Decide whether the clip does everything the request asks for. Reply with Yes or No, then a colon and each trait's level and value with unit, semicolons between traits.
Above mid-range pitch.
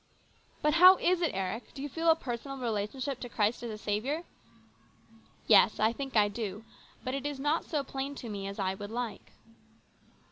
Yes: high, 245 Hz